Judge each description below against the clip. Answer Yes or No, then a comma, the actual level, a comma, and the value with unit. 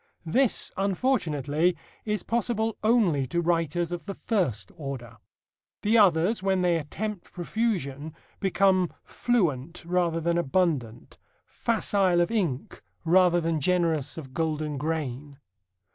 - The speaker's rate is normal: No, slow, 115 wpm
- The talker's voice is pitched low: No, medium, 170 Hz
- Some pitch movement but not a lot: Yes, average, 4.5 semitones